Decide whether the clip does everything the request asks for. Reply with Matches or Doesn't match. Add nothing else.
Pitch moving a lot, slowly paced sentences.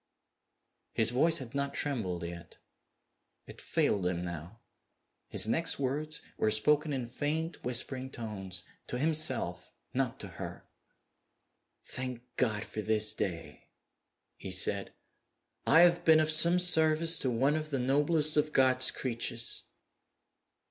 Matches